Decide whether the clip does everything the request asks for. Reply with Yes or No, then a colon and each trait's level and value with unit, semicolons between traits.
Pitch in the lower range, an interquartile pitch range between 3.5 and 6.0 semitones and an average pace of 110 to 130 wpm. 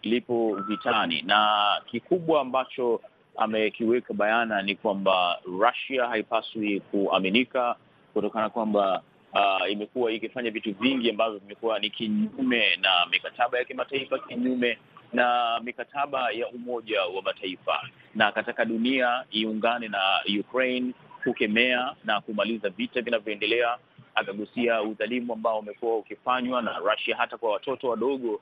No: low, 115 Hz; narrow, 2.6 semitones; average, 120 wpm